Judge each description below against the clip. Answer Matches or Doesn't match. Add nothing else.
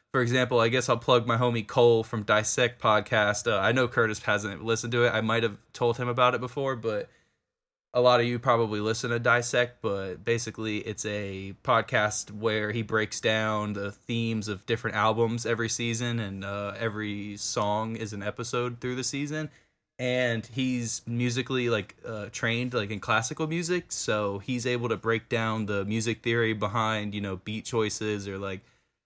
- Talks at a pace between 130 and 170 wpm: Doesn't match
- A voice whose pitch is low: Matches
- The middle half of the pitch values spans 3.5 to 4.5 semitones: Doesn't match